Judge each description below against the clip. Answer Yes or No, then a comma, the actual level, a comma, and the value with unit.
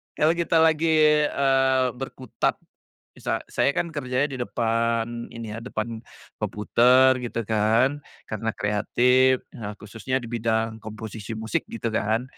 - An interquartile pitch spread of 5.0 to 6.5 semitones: No, average, 2.8 semitones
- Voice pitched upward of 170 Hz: No, low, 115 Hz